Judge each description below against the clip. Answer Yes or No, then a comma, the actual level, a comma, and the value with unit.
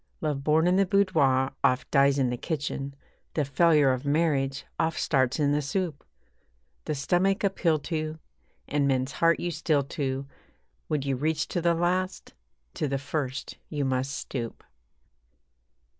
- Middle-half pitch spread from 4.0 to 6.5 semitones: No, average, 3.3 semitones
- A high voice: No, medium, 145 Hz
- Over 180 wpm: No, average, 155 wpm